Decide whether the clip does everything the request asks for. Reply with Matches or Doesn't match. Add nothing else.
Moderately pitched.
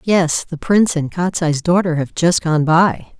Matches